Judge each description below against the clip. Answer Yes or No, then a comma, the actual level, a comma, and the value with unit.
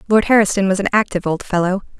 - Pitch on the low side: No, high, 195 Hz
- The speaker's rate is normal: No, fast, 210 wpm